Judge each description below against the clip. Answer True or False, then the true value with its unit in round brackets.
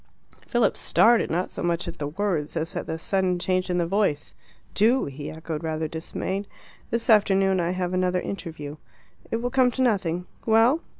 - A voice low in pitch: False (185 Hz)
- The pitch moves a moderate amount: True (4.3 semitones)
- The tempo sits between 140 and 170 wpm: False (180 wpm)